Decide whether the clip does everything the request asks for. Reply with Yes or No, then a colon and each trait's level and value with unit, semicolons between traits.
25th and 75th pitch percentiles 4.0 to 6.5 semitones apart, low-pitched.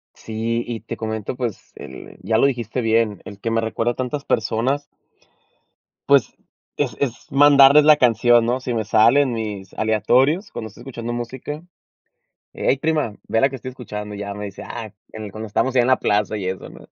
No: average, 3.3 semitones; low, 115 Hz